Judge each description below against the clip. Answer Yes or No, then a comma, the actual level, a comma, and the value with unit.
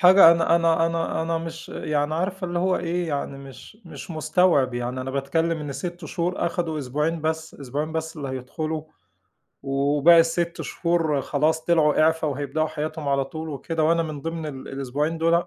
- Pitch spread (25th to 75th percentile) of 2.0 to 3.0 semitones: Yes, narrow, 2.6 semitones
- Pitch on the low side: No, medium, 160 Hz